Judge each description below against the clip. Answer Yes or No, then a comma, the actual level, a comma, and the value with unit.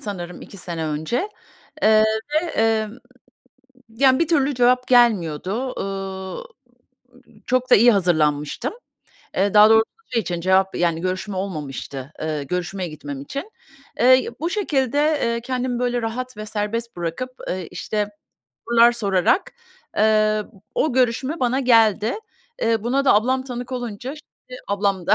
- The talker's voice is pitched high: Yes, high, 220 Hz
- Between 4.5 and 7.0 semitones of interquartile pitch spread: Yes, average, 5.1 semitones